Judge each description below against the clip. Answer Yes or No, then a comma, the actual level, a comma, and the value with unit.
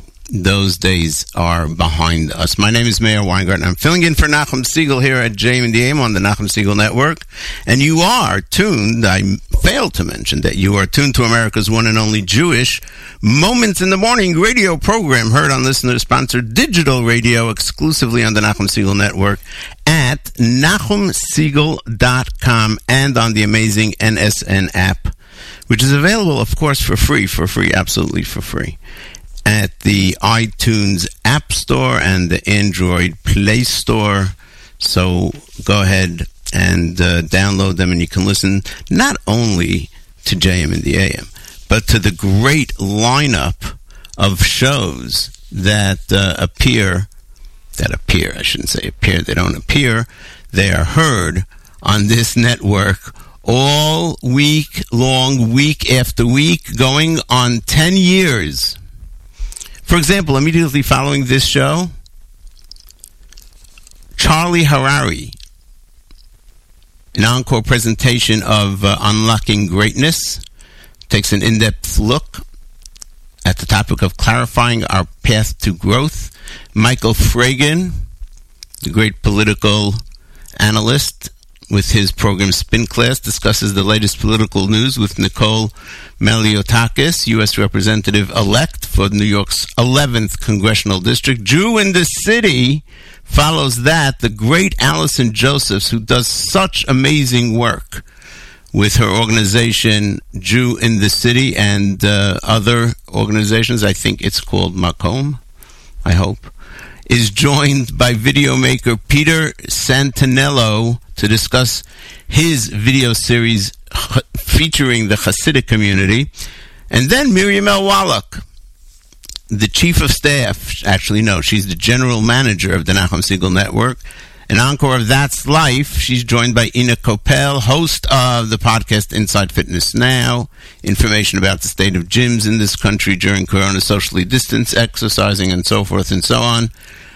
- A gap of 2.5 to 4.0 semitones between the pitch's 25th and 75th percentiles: No, average, 4.8 semitones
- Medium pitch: No, low, 110 Hz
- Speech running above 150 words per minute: No, slow, 135 wpm